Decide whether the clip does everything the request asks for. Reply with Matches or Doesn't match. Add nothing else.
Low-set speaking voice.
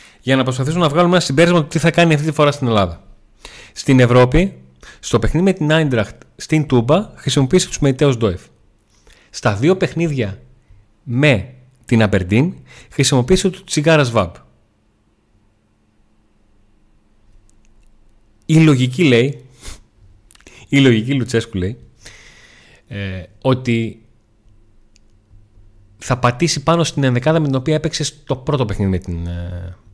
Matches